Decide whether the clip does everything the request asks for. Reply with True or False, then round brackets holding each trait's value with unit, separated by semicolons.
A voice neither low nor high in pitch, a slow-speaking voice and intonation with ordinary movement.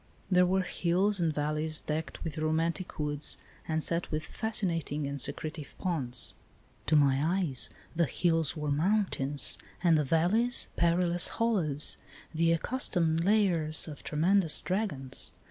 True (165 Hz; 130 wpm; 3.2 semitones)